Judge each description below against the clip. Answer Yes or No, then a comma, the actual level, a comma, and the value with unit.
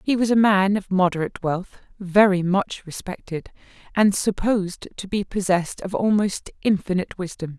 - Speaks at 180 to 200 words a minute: No, average, 150 wpm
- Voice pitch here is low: No, high, 190 Hz